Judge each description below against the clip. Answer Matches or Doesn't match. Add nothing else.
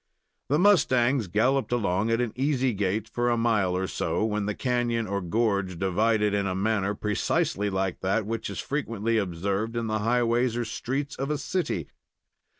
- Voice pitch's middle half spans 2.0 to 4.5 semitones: Matches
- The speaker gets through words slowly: Doesn't match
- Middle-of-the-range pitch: Doesn't match